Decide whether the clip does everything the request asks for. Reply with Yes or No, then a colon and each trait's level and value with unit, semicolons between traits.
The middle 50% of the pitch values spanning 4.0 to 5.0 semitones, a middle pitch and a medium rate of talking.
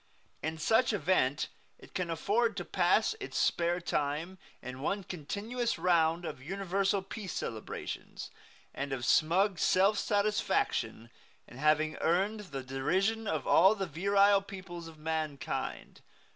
No: average, 4.4 semitones; medium, 180 Hz; slow, 130 wpm